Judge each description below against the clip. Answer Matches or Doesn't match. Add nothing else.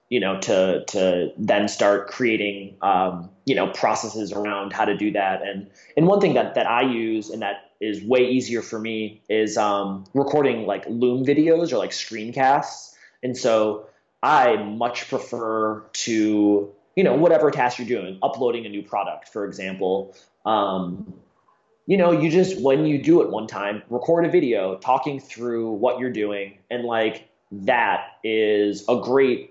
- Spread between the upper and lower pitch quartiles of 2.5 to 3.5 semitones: Doesn't match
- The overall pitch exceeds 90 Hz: Matches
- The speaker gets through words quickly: Doesn't match